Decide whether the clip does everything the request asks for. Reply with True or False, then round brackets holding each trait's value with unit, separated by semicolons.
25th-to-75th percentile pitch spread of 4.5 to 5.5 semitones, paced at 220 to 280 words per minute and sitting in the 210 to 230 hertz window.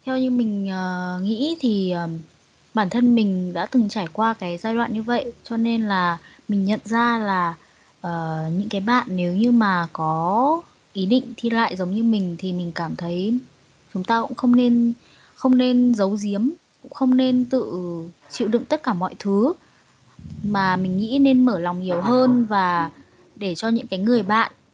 False (4.8 semitones; 190 wpm; 215 Hz)